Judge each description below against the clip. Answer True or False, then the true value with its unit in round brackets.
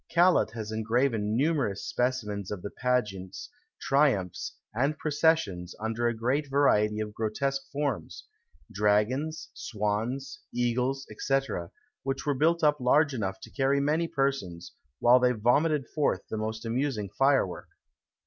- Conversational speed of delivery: False (130 wpm)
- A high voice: False (125 Hz)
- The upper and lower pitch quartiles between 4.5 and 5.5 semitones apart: True (4.9 semitones)